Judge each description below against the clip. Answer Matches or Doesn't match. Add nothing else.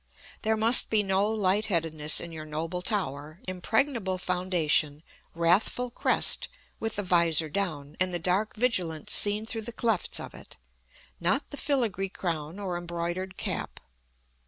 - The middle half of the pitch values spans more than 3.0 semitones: Matches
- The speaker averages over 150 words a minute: Doesn't match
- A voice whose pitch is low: Doesn't match